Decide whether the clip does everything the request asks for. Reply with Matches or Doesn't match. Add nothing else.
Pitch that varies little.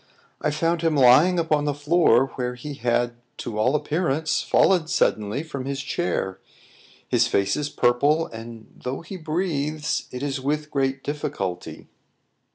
Doesn't match